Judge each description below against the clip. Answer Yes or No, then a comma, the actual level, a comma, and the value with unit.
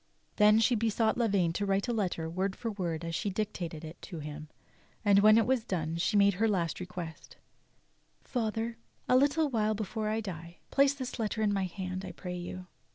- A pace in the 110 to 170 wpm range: No, average, 200 wpm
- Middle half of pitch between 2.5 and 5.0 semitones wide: Yes, average, 4.1 semitones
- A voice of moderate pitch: No, high, 200 Hz